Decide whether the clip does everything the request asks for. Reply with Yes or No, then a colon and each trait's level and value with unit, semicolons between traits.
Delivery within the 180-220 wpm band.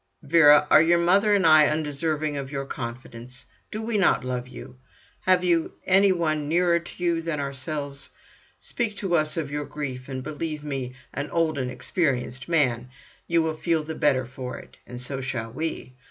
Yes: average, 185 wpm